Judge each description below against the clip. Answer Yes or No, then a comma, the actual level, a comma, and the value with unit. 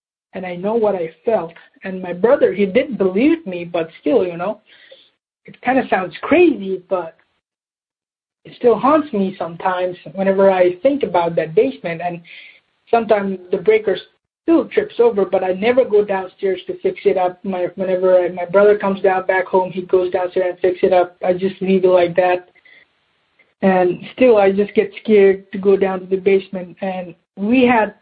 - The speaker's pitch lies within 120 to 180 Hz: No, high, 190 Hz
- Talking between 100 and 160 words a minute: No, average, 185 wpm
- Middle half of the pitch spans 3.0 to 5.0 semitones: No, narrow, 2.5 semitones